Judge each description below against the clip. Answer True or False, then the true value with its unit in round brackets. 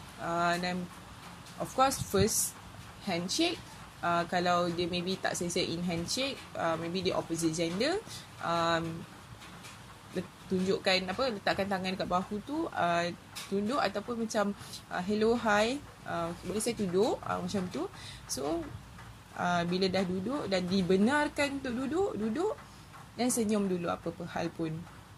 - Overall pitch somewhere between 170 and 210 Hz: True (185 Hz)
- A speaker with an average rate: True (140 wpm)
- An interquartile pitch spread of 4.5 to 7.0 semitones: False (4.0 semitones)